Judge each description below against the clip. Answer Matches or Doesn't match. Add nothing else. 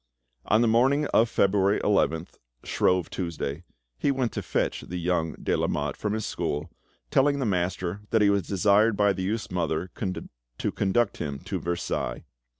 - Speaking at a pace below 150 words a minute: Doesn't match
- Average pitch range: Matches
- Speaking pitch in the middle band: Doesn't match